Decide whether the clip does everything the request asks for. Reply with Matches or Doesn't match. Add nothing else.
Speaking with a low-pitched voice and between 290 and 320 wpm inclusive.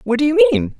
Doesn't match